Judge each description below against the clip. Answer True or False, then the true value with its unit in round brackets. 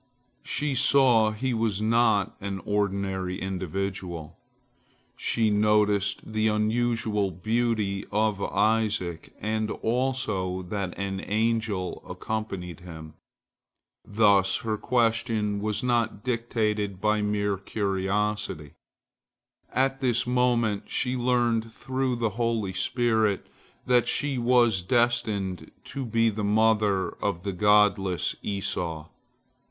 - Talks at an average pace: False (105 wpm)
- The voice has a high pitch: False (105 Hz)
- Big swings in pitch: False (3.0 semitones)